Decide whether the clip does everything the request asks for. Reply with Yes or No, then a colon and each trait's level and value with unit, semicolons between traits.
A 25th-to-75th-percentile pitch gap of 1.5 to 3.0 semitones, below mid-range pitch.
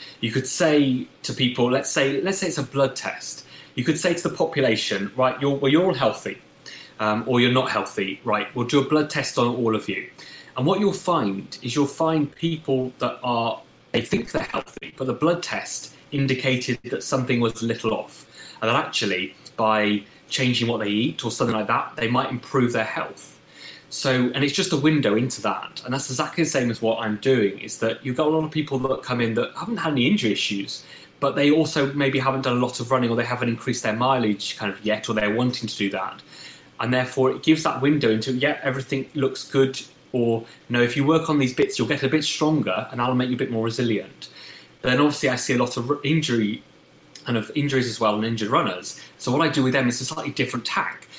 No: average, 3.4 semitones; low, 130 Hz